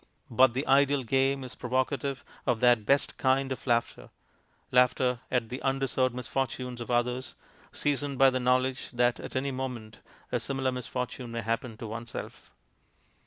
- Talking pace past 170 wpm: No, average, 155 wpm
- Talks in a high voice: No, low, 125 Hz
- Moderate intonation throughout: No, narrow, 1.8 semitones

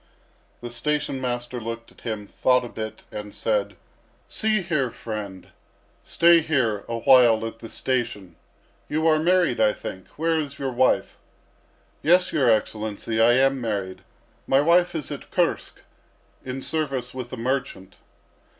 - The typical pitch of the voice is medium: No, low, 125 Hz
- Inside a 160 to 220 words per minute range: No, average, 150 wpm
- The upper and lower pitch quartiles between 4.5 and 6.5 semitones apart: Yes, average, 5.0 semitones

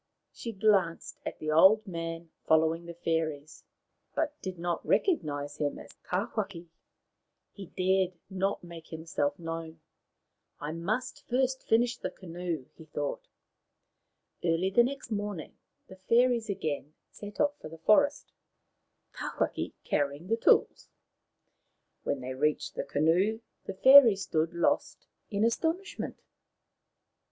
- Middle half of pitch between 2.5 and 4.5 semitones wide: No, average, 5.2 semitones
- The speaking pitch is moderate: Yes, medium, 180 Hz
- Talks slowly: Yes, slow, 125 wpm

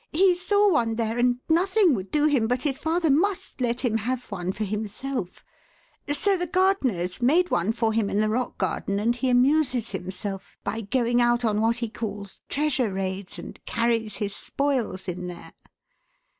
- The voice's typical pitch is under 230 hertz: No, high, 240 Hz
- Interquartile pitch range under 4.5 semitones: No, wide, 5.5 semitones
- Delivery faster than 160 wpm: Yes, average, 180 wpm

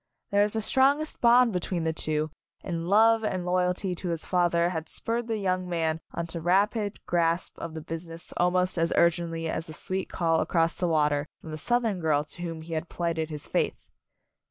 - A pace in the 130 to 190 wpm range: No, fast, 205 wpm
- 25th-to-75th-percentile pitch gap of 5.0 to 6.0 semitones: No, average, 2.8 semitones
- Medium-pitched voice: Yes, medium, 175 Hz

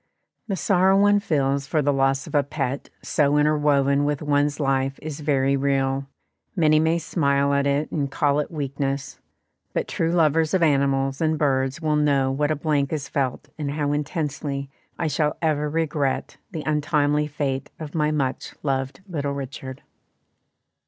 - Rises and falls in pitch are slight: Yes, narrow, 1.9 semitones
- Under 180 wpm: Yes, average, 165 wpm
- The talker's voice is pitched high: No, medium, 145 Hz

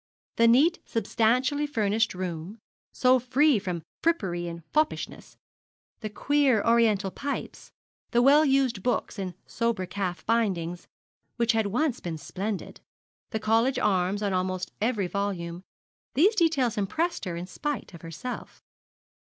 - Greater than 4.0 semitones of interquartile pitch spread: Yes, wide, 5.6 semitones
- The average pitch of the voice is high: Yes, high, 220 Hz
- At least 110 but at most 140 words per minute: Yes, slow, 135 wpm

